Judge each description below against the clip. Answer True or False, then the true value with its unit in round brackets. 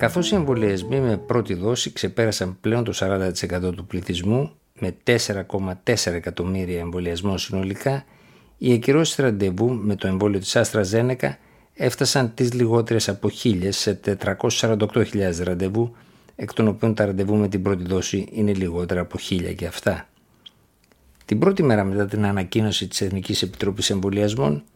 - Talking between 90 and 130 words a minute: False (145 wpm)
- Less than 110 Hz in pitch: True (100 Hz)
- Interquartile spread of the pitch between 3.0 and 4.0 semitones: True (3.5 semitones)